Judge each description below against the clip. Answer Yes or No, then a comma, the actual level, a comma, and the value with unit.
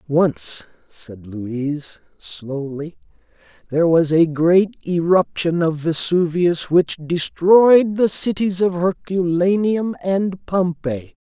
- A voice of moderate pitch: Yes, medium, 165 Hz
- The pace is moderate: No, slow, 100 wpm